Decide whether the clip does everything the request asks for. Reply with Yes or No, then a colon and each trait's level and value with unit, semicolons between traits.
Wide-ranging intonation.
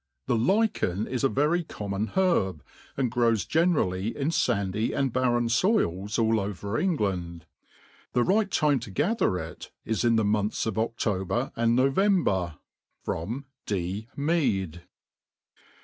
Yes: wide, 6.3 semitones